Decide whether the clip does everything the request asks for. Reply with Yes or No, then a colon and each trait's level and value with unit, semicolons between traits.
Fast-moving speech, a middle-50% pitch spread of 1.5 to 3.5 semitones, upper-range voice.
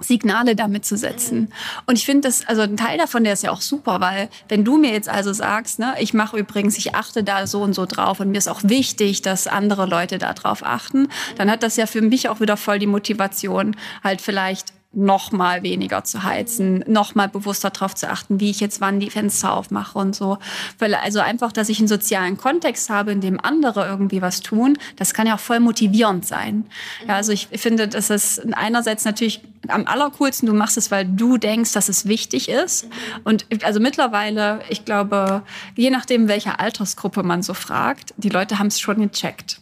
Yes: fast, 210 wpm; narrow, 2.4 semitones; high, 210 Hz